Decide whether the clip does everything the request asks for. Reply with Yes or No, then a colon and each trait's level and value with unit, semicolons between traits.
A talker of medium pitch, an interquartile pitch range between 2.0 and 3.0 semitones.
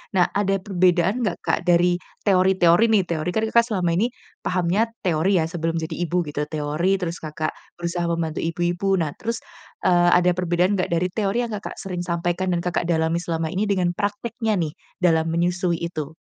Yes: medium, 175 Hz; narrow, 2.4 semitones